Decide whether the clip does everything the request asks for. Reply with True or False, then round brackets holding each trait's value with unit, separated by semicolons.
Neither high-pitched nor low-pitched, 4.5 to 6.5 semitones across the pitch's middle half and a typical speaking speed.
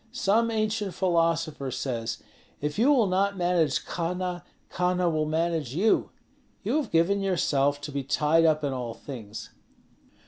True (165 Hz; 4.8 semitones; 145 wpm)